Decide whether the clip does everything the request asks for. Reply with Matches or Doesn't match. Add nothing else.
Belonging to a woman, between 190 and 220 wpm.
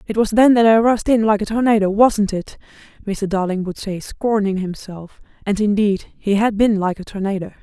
Matches